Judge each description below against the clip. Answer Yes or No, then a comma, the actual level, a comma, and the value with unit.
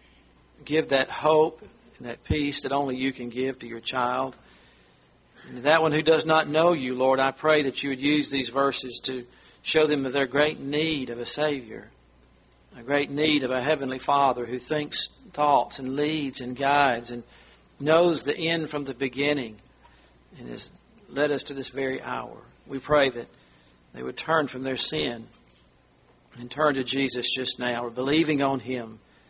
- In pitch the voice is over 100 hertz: Yes, low, 135 Hz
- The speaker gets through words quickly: No, average, 180 wpm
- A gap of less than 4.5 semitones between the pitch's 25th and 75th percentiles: Yes, average, 3.5 semitones